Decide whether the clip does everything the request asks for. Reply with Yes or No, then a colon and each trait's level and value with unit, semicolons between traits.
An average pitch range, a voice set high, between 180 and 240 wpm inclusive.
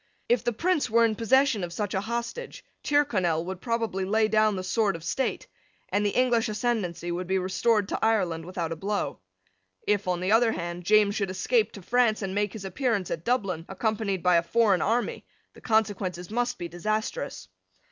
Yes: average, 3.9 semitones; high, 210 Hz; average, 190 wpm